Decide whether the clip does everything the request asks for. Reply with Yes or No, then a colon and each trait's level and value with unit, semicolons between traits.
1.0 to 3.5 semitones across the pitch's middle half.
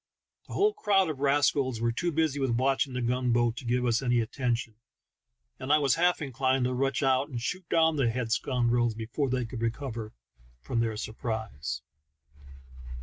Yes: average, 3.2 semitones